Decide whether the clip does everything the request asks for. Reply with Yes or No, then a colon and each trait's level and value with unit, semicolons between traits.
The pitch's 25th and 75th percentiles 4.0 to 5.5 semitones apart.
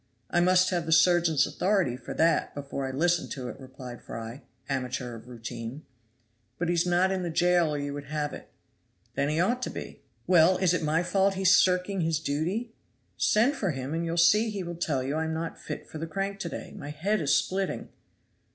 Yes: average, 4.4 semitones